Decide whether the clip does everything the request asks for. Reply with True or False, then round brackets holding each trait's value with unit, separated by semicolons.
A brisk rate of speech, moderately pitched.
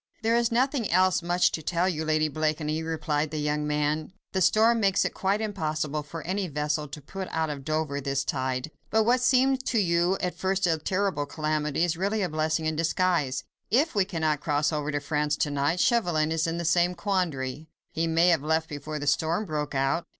True (210 wpm; 160 Hz)